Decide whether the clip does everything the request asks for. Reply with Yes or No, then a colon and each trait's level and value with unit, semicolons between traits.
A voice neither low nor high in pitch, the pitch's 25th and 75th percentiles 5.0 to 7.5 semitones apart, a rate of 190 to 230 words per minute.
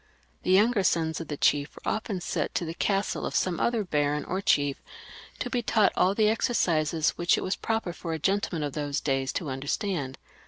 Yes: medium, 170 Hz; average, 5.3 semitones; fast, 205 wpm